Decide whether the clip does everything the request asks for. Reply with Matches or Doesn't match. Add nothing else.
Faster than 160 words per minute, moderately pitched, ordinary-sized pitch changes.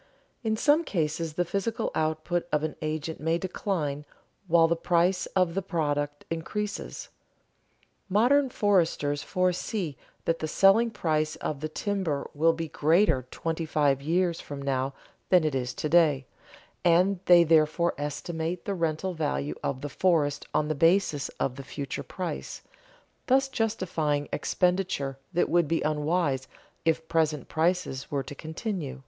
Doesn't match